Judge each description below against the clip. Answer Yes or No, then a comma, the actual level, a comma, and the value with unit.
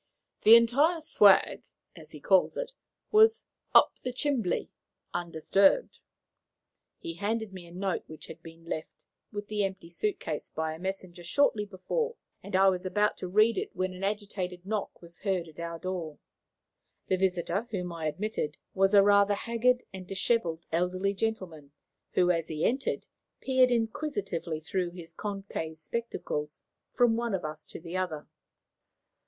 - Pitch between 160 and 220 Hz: Yes, high, 190 Hz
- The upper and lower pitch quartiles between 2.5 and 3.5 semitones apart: No, average, 4.3 semitones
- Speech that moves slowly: No, average, 160 wpm